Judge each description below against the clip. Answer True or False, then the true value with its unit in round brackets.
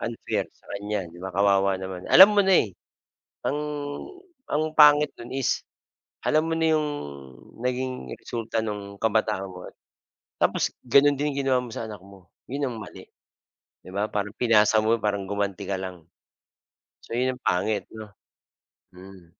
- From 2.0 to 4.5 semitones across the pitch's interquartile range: False (4.9 semitones)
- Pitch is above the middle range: False (110 Hz)